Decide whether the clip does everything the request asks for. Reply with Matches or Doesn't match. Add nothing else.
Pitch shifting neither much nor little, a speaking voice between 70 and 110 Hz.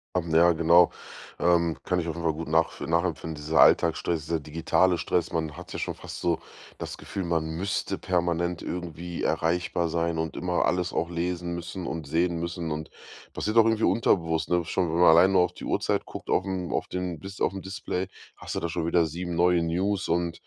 Doesn't match